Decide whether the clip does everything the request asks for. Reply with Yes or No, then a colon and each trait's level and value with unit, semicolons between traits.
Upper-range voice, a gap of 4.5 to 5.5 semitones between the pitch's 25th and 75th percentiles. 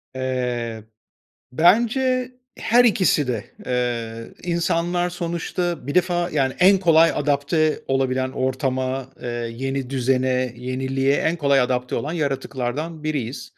No: medium, 140 Hz; average, 4.9 semitones